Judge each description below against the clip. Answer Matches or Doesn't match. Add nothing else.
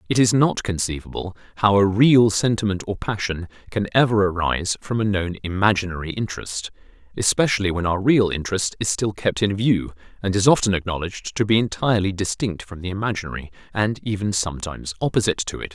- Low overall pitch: Matches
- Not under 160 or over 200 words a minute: Matches